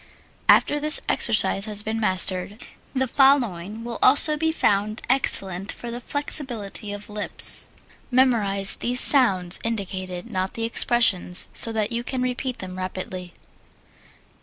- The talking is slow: Yes, slow, 130 wpm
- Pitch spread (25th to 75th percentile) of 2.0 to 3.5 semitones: No, average, 4.7 semitones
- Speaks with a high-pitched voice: Yes, high, 220 Hz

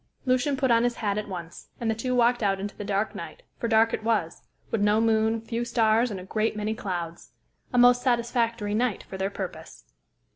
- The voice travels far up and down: No, average, 2.8 semitones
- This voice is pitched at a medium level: No, high, 225 Hz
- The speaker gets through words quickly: Yes, fast, 215 wpm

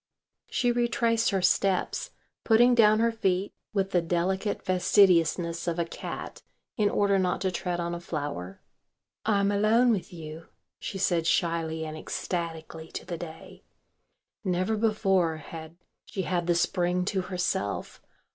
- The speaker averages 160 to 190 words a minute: No, average, 145 wpm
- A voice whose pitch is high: No, medium, 180 Hz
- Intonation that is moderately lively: Yes, average, 3.4 semitones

